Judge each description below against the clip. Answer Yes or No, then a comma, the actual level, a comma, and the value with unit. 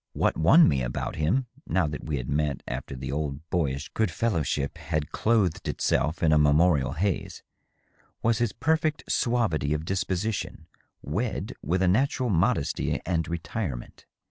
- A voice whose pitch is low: Yes, very low, 80 Hz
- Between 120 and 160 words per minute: Yes, average, 150 wpm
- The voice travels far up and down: Yes, wide, 6.7 semitones